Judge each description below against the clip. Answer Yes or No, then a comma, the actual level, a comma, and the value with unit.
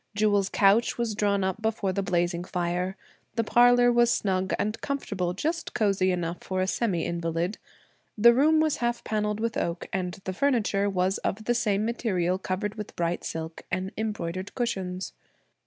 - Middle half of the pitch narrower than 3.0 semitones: No, average, 3.8 semitones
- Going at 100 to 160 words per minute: No, average, 170 wpm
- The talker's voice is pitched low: No, high, 200 Hz